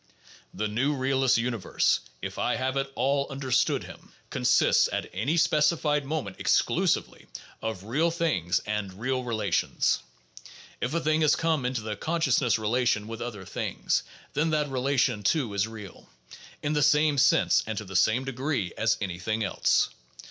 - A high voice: No, low, 125 Hz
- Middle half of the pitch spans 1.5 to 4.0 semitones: No, wide, 5.6 semitones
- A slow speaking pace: No, average, 165 wpm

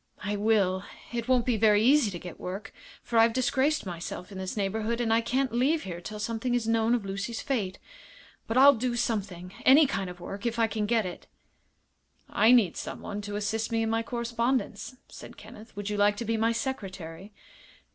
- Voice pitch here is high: Yes, high, 225 Hz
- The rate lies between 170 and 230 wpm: Yes, average, 200 wpm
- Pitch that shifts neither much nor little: Yes, average, 3.0 semitones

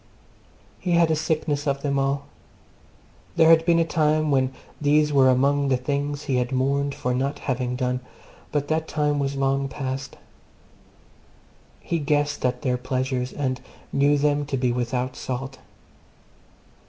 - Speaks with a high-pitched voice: No, medium, 140 Hz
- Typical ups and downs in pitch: No, narrow, 2.2 semitones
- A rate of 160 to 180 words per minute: No, average, 150 wpm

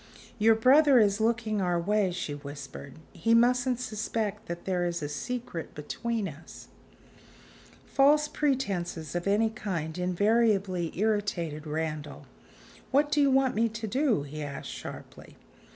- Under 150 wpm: Yes, slow, 135 wpm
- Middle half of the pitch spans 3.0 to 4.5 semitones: No, wide, 5.6 semitones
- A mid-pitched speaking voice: No, high, 205 Hz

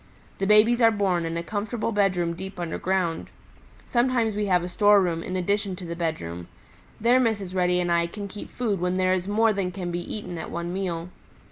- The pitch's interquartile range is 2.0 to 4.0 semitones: Yes, average, 3.1 semitones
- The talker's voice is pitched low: No, medium, 185 Hz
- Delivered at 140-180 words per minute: No, fast, 205 wpm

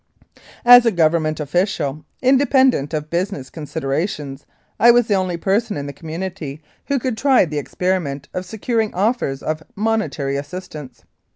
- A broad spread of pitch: Yes, wide, 6.8 semitones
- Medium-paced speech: Yes, average, 145 wpm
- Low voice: No, medium, 175 Hz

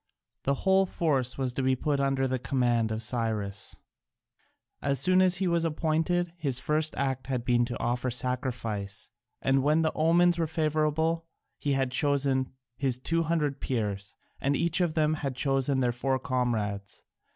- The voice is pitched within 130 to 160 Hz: Yes, low, 135 Hz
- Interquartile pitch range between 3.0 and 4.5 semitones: Yes, average, 4.1 semitones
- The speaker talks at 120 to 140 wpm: No, average, 165 wpm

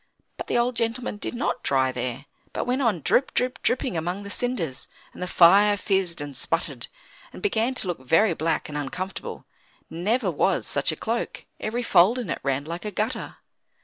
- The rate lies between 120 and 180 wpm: No, average, 190 wpm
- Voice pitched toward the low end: No, high, 195 Hz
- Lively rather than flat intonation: Yes, wide, 6.8 semitones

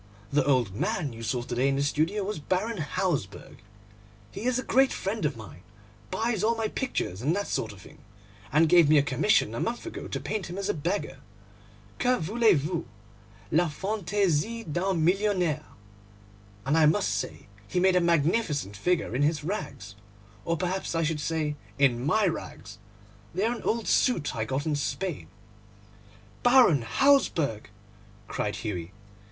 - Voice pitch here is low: No, medium, 160 Hz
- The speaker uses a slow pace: No, average, 170 wpm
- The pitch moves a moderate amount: No, wide, 6.5 semitones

